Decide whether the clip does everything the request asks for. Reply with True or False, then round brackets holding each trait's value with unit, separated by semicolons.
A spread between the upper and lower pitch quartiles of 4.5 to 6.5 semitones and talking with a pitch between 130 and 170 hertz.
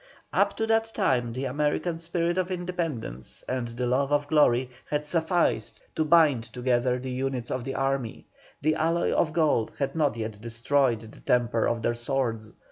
True (5.0 semitones; 135 Hz)